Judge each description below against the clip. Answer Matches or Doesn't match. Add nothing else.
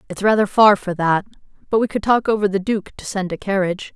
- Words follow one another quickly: Matches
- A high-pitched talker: Matches